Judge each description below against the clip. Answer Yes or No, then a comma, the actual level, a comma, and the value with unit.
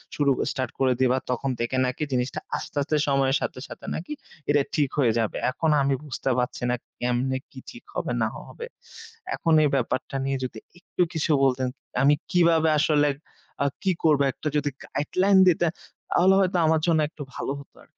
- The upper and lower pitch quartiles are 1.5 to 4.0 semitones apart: Yes, average, 3.7 semitones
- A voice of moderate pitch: Yes, medium, 145 Hz